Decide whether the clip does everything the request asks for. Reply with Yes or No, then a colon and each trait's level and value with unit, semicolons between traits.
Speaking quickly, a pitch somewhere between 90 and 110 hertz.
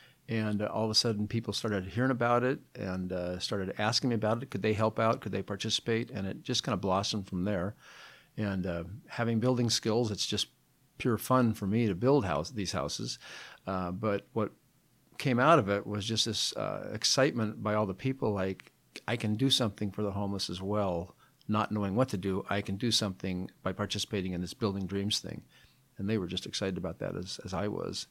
Yes: fast, 215 wpm; low, 105 Hz